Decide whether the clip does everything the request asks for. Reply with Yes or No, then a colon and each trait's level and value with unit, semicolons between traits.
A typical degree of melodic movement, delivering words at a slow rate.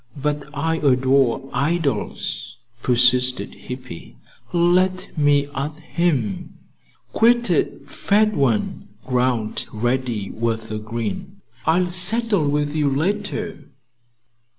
No: wide, 5.9 semitones; slow, 100 wpm